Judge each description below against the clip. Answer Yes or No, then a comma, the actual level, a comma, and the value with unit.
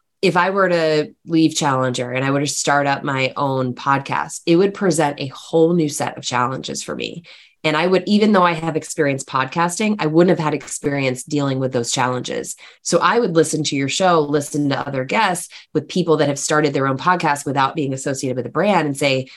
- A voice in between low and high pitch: Yes, medium, 150 Hz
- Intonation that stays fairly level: No, average, 3.8 semitones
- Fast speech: Yes, fast, 220 wpm